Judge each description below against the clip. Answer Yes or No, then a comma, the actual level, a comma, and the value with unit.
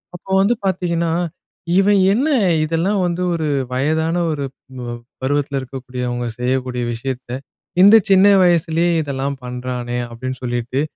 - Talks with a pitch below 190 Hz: Yes, medium, 140 Hz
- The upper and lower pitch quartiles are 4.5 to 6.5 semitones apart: Yes, wide, 5.5 semitones